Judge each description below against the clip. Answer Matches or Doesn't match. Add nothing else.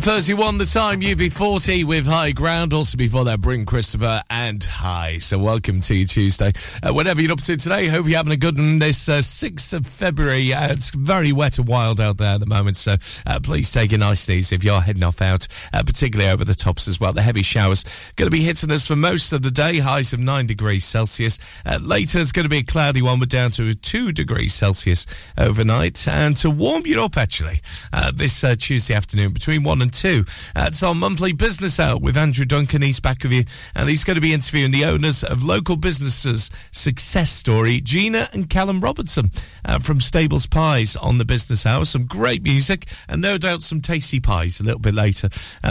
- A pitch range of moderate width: Doesn't match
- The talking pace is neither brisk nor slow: Doesn't match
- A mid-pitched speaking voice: Doesn't match